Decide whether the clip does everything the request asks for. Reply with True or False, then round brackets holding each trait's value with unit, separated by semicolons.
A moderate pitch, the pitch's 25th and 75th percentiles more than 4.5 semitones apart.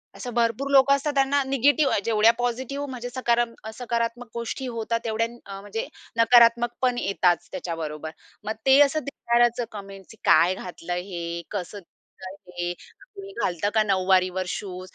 False (230 Hz; 4.9 semitones)